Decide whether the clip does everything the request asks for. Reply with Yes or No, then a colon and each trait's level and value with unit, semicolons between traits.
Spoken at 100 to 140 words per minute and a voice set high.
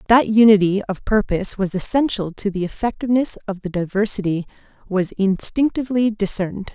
Yes: slow, 135 wpm; high, 205 Hz